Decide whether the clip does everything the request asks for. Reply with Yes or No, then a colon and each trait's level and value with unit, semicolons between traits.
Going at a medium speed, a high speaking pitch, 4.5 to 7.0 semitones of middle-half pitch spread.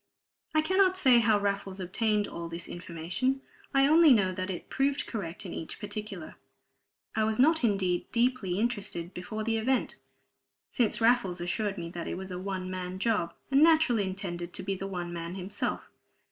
Yes: average, 175 wpm; high, 200 Hz; average, 4.9 semitones